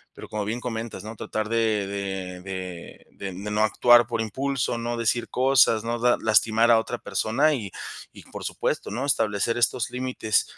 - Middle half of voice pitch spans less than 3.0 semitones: Yes, narrow, 2.5 semitones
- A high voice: No, low, 115 Hz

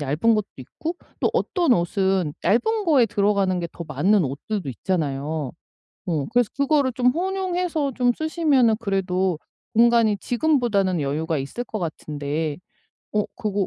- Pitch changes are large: Yes, wide, 7.5 semitones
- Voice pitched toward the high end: Yes, high, 205 Hz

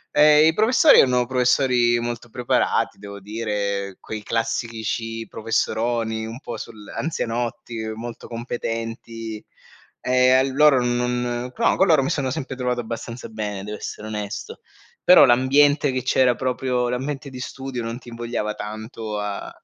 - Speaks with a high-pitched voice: No, low, 120 Hz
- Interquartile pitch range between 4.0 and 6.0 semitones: No, narrow, 2.6 semitones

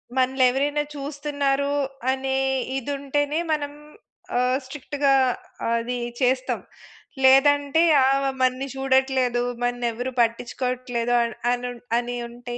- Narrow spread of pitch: Yes, narrow, 2.2 semitones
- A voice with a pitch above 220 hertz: Yes, very high, 265 Hz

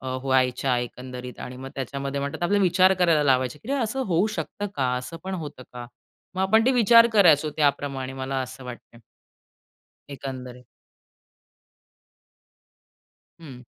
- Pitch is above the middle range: No, medium, 140 Hz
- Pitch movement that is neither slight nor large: No, wide, 6.4 semitones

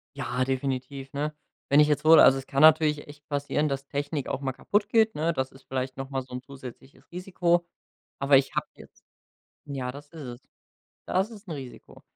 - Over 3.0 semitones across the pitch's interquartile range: No, narrow, 2.6 semitones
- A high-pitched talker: No, medium, 140 Hz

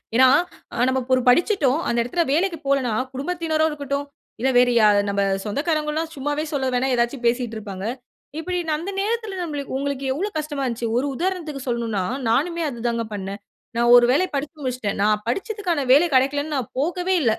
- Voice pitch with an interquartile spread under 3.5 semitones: No, average, 5.0 semitones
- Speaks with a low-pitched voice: No, very high, 275 Hz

